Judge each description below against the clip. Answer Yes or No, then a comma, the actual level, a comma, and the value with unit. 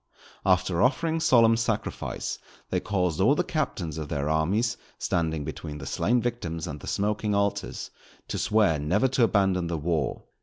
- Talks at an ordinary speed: Yes, average, 160 wpm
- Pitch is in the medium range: No, very low, 95 Hz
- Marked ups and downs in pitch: Yes, wide, 6.1 semitones